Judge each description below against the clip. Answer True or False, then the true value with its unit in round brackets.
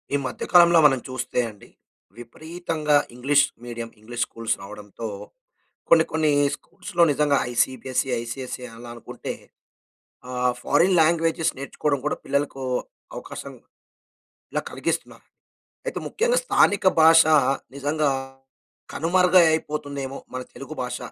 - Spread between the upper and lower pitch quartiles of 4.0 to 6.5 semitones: True (4.6 semitones)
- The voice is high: False (145 Hz)